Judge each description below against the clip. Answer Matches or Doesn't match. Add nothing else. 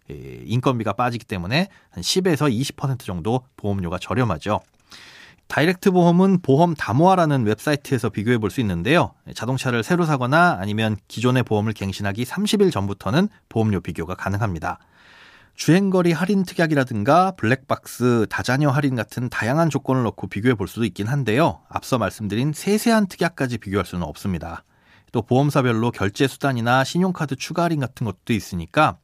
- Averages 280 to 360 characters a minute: Doesn't match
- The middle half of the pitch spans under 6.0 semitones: Doesn't match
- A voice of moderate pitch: Doesn't match